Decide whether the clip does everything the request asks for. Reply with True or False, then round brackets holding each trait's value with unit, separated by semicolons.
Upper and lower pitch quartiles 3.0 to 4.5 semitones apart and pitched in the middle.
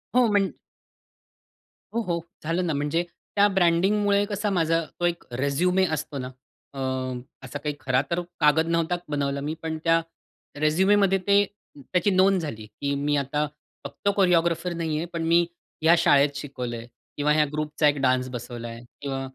True (4.0 semitones; 160 Hz)